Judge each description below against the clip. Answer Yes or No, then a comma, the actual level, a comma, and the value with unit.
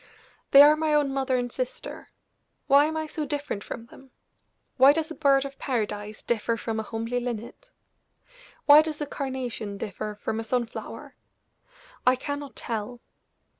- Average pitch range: Yes, average, 4.3 semitones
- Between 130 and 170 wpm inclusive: Yes, average, 165 wpm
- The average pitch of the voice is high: Yes, very high, 260 Hz